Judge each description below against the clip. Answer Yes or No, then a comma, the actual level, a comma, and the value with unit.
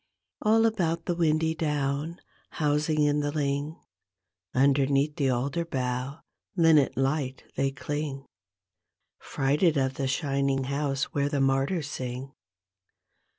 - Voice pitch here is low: No, medium, 145 Hz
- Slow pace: Yes, slow, 115 wpm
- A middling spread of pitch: No, narrow, 2.3 semitones